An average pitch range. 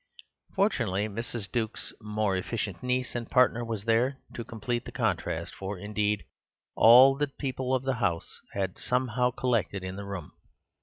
Yes: average, 3.9 semitones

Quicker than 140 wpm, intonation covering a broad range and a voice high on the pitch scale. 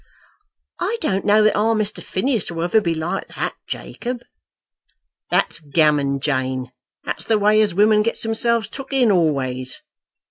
Yes: average, 150 wpm; wide, 6.7 semitones; high, 205 Hz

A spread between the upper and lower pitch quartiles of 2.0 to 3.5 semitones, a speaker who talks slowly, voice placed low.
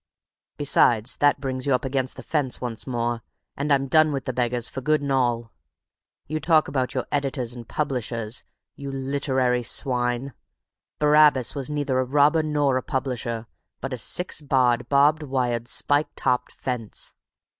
No: average, 2.8 semitones; average, 160 wpm; low, 130 Hz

